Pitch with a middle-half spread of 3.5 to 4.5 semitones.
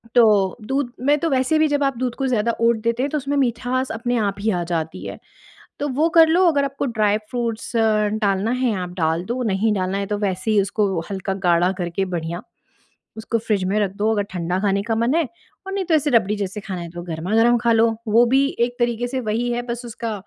Yes: average, 4.1 semitones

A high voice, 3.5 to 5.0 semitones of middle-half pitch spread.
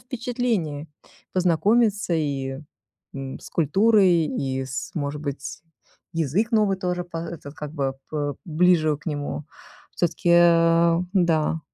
No: medium, 165 Hz; average, 3.9 semitones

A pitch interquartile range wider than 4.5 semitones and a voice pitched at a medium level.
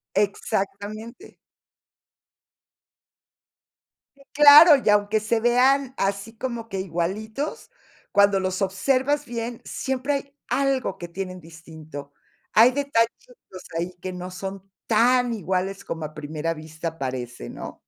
No: wide, 5.6 semitones; high, 205 Hz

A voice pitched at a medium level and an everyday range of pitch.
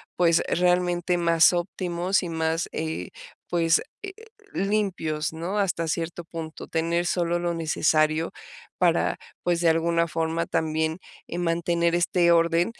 No: medium, 170 Hz; narrow, 1.3 semitones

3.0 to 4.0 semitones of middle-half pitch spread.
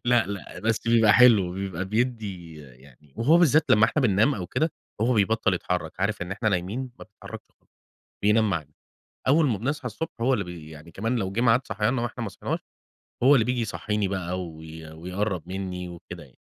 No: average, 4.7 semitones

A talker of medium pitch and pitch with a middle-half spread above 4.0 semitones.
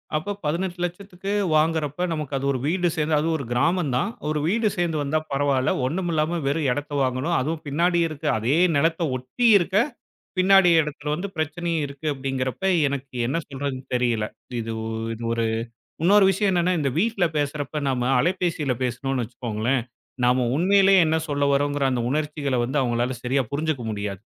Yes: medium, 150 Hz; average, 4.7 semitones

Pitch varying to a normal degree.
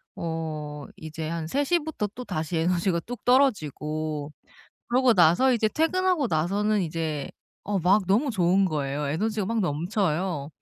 No: wide, 6.1 semitones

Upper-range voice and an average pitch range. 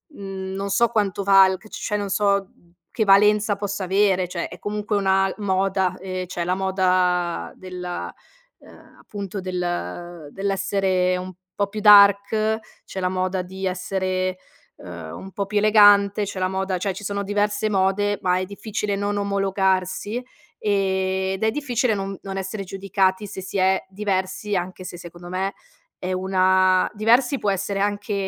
No: high, 195 Hz; narrow, 1.5 semitones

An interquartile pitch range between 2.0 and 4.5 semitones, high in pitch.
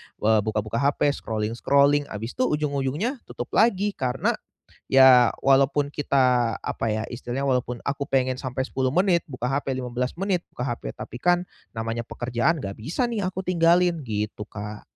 No: average, 3.7 semitones; low, 130 Hz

